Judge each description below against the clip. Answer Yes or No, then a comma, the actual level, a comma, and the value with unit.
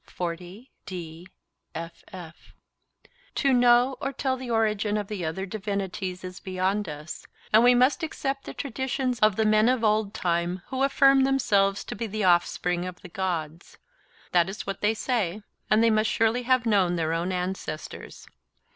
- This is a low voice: No, high, 210 Hz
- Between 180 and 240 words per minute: No, average, 150 wpm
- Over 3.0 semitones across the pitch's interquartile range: Yes, average, 5.2 semitones